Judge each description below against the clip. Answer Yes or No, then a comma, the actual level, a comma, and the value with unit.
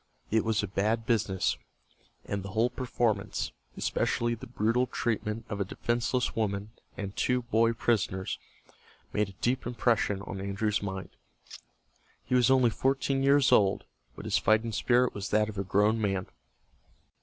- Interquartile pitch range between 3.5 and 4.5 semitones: No, average, 3.0 semitones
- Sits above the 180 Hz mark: No, low, 110 Hz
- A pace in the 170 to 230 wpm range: No, average, 155 wpm